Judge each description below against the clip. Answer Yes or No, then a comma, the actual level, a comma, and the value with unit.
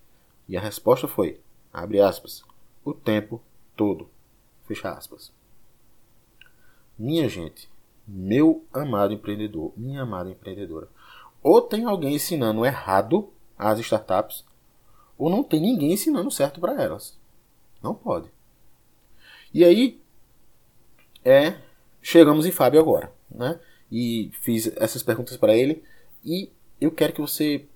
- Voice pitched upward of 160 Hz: No, low, 120 Hz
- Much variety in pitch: Yes, wide, 7.2 semitones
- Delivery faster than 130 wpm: No, slow, 120 wpm